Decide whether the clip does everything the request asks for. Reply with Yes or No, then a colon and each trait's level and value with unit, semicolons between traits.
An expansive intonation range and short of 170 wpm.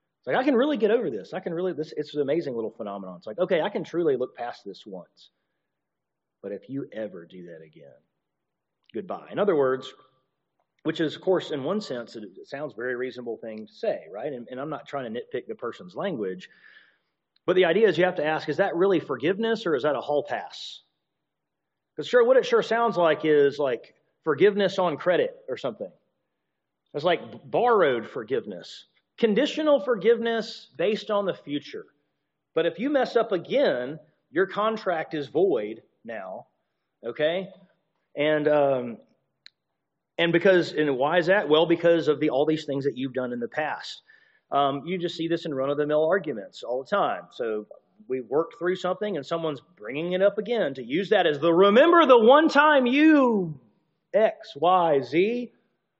No: wide, 7.7 semitones; average, 185 wpm